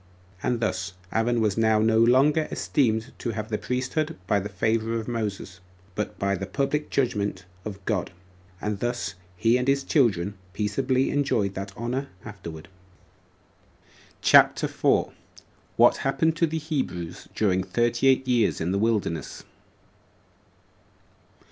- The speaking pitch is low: Yes, low, 115 Hz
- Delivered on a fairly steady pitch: No, average, 4.5 semitones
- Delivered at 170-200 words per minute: No, slow, 135 wpm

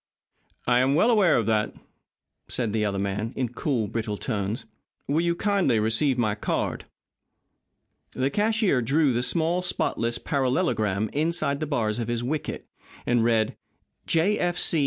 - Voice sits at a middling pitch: No, low, 125 Hz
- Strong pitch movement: Yes, wide, 6.3 semitones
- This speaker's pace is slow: No, average, 155 wpm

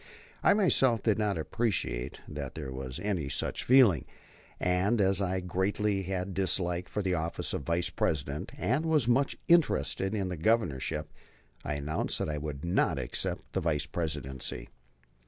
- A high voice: No, very low, 90 Hz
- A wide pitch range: Yes, wide, 5.8 semitones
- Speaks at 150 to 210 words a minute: Yes, average, 155 wpm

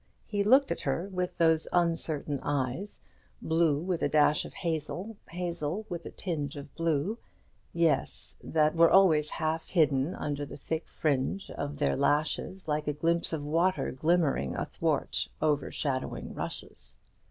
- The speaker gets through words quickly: No, average, 145 wpm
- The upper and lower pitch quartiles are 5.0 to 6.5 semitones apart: No, average, 3.1 semitones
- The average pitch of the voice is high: No, medium, 160 Hz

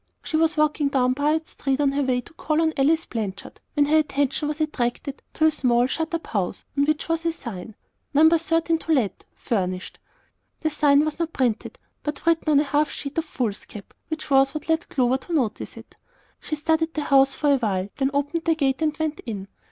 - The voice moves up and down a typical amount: Yes, average, 3.5 semitones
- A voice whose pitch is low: No, very high, 290 Hz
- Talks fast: Yes, fast, 210 wpm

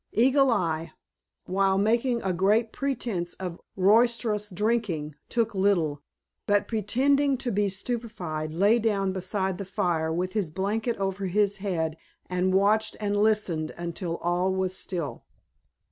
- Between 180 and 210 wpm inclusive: No, slow, 135 wpm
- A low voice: No, high, 195 Hz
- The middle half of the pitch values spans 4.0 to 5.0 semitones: No, average, 3.6 semitones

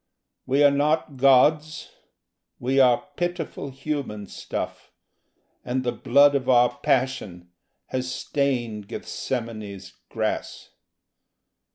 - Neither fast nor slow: No, slow, 95 wpm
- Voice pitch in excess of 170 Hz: No, low, 130 Hz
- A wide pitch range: No, average, 2.7 semitones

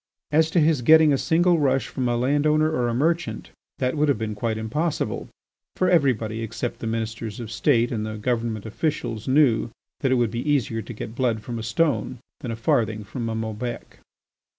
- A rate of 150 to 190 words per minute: No, average, 200 wpm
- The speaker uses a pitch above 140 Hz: No, low, 120 Hz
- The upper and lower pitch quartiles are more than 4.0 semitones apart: Yes, average, 4.7 semitones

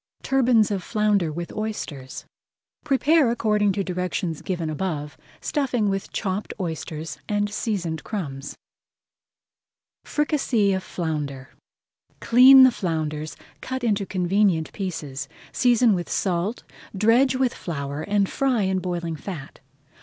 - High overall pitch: Yes, high, 195 Hz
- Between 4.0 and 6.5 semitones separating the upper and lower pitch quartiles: Yes, wide, 5.6 semitones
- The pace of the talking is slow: Yes, slow, 115 wpm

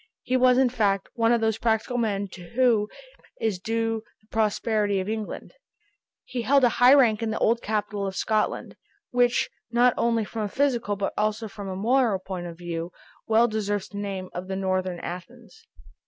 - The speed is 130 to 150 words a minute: No, average, 185 wpm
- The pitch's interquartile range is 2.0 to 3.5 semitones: Yes, average, 3.1 semitones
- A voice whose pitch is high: Yes, high, 215 Hz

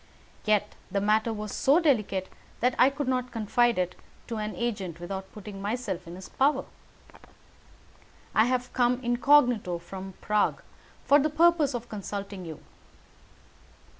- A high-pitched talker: Yes, high, 220 Hz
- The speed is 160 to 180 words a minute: No, average, 140 wpm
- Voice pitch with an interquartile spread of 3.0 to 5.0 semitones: Yes, average, 4.4 semitones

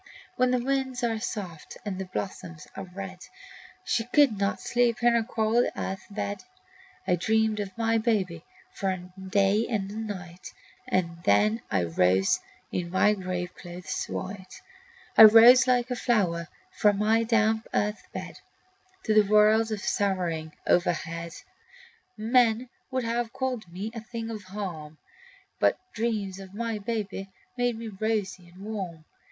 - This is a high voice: Yes, high, 210 Hz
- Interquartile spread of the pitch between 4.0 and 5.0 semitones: No, average, 3.6 semitones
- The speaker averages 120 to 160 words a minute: Yes, average, 150 wpm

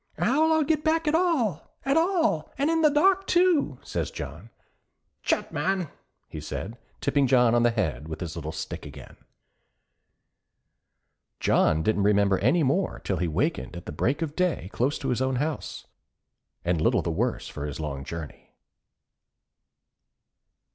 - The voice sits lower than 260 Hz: Yes, low, 135 Hz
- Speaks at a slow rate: No, average, 160 wpm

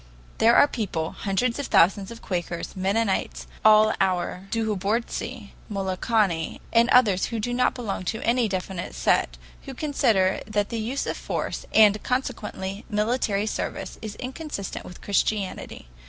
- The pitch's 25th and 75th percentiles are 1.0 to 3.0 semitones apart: No, average, 3.4 semitones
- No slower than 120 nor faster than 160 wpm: Yes, average, 140 wpm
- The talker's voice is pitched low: No, high, 210 Hz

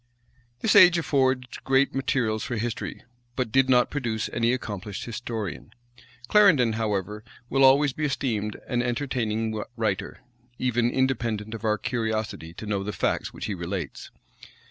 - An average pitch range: Yes, average, 3.6 semitones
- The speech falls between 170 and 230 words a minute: No, average, 145 wpm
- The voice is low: Yes, low, 115 Hz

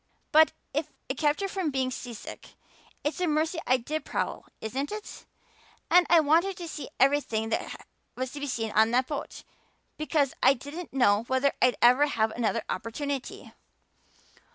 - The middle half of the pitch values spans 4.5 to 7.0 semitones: No, average, 4.1 semitones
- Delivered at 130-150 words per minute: No, average, 165 wpm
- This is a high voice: Yes, very high, 280 Hz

